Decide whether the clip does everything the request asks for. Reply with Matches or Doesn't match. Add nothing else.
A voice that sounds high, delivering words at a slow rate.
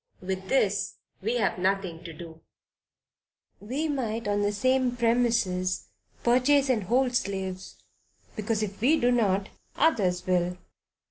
Matches